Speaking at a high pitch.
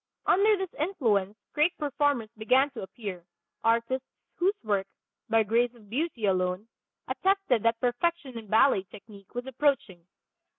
Yes: high, 240 Hz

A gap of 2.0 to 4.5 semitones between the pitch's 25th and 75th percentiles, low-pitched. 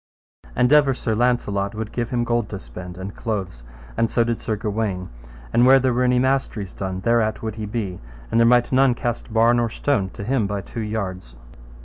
Yes: average, 3.3 semitones; low, 115 Hz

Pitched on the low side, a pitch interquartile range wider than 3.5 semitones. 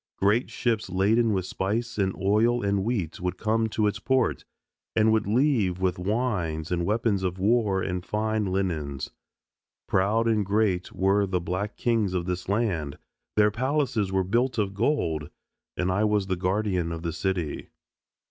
No: low, 100 Hz; average, 3.2 semitones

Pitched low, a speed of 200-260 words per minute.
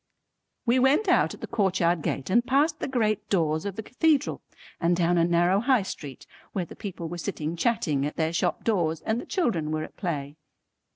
No: medium, 180 Hz; fast, 205 wpm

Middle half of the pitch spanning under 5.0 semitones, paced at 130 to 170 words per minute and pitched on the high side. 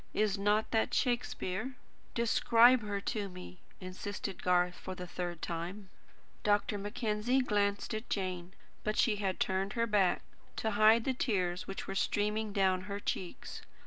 Yes: average, 2.8 semitones; average, 150 wpm; high, 205 Hz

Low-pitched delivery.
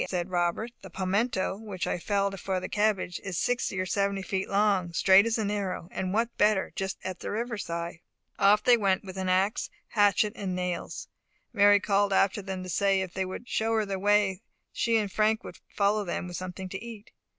No: high, 195 Hz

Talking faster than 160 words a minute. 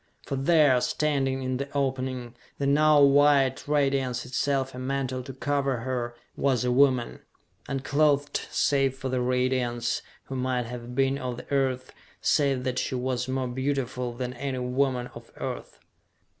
No: average, 155 wpm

